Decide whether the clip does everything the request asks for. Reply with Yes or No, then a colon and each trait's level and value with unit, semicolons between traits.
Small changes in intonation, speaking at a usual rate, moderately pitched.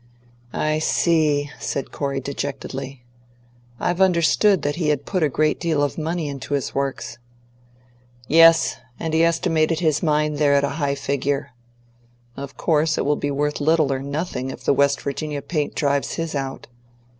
Yes: narrow, 2.3 semitones; average, 165 wpm; medium, 145 Hz